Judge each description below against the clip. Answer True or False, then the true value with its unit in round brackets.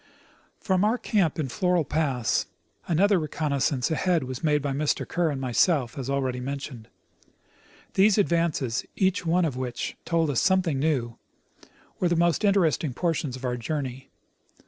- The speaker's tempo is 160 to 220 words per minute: False (150 wpm)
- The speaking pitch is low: False (155 Hz)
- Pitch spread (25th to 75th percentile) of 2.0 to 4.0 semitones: False (4.8 semitones)